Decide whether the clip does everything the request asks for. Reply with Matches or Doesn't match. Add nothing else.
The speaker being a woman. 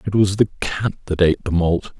Doesn't match